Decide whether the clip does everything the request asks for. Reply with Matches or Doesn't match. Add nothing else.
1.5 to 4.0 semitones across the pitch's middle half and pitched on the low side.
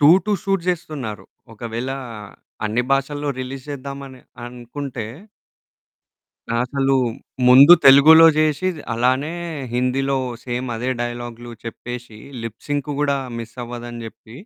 Matches